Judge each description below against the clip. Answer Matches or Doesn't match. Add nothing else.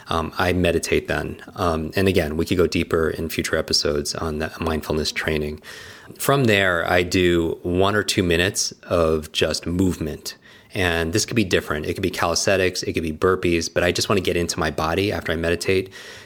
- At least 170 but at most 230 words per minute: Matches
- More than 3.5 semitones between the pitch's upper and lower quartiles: Doesn't match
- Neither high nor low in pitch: Doesn't match